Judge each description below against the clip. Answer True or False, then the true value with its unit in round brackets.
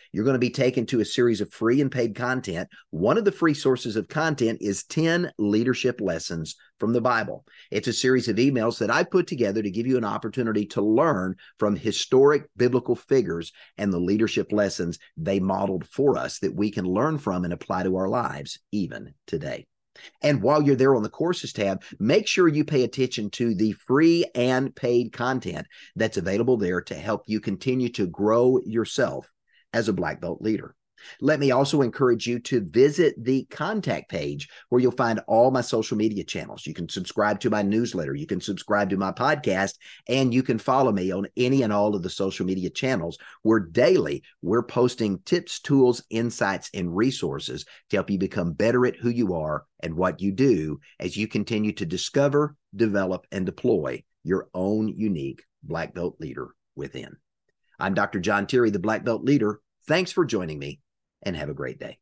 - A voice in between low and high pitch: False (115 Hz)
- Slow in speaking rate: False (195 wpm)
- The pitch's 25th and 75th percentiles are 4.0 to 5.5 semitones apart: True (4.4 semitones)